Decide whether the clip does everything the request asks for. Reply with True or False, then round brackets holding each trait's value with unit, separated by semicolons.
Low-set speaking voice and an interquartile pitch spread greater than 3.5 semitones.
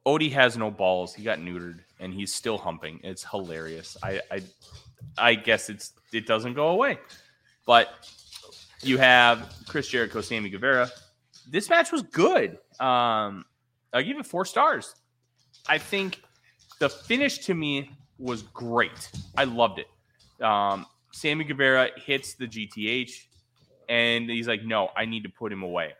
True (120 Hz; 3.9 semitones)